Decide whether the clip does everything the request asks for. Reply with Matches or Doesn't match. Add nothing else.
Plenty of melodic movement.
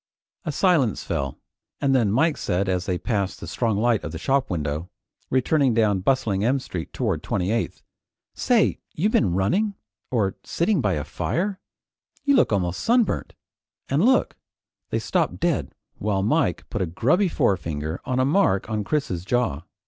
Matches